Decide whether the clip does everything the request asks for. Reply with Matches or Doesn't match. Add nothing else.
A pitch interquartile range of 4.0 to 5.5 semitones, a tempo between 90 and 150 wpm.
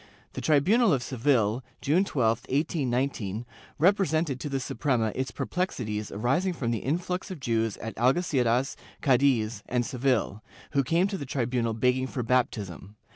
Matches